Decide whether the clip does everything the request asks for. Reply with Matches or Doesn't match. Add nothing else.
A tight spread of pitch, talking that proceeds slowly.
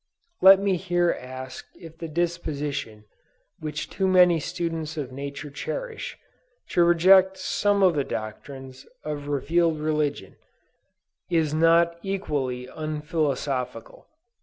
Doesn't match